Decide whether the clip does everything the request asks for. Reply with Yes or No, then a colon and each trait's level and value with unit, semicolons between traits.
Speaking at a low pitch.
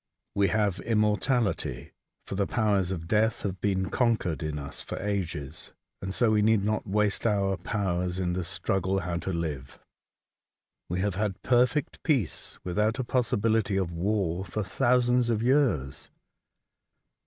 Yes: low, 100 Hz